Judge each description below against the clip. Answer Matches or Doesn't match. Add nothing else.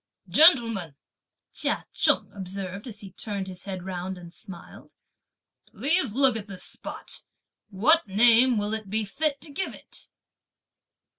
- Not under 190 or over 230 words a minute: Doesn't match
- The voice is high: Matches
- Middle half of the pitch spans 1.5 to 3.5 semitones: Doesn't match